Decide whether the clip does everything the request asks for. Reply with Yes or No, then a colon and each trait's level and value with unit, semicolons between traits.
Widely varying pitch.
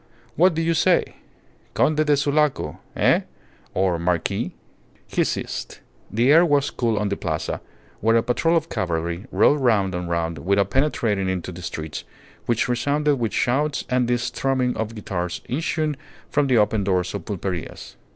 Yes: wide, 7.6 semitones